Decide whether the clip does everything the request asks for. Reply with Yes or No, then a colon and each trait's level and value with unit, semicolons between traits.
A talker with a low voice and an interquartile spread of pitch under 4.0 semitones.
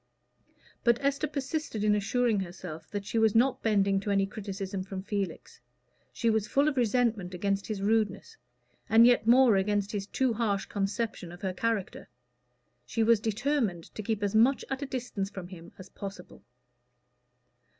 No: high, 210 Hz; average, 3.3 semitones